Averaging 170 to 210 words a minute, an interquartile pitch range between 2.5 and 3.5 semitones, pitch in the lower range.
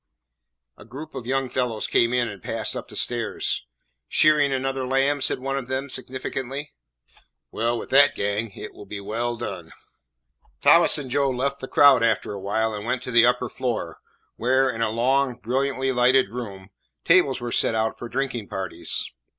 Yes: average, 180 wpm; average, 2.9 semitones; low, 125 Hz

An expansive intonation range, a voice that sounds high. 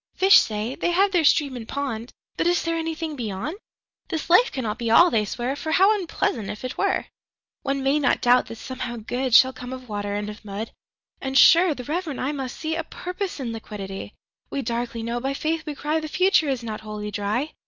Yes: wide, 5.8 semitones; very high, 260 Hz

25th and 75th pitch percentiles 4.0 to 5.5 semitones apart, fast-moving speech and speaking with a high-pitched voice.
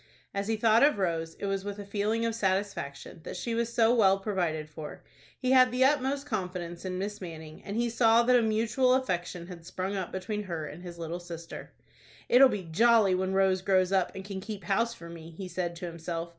Yes: average, 4.6 semitones; fast, 220 wpm; high, 195 Hz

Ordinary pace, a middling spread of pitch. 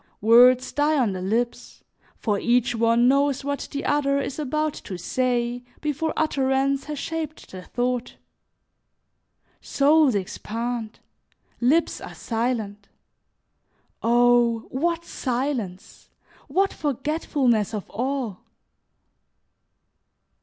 No: slow, 100 wpm; average, 3.7 semitones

